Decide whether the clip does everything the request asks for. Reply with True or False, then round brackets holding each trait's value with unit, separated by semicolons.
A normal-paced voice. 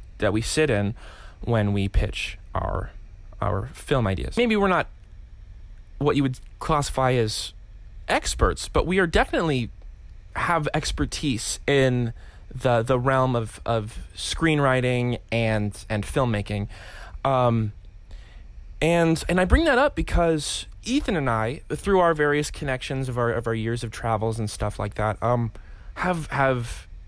True (145 wpm)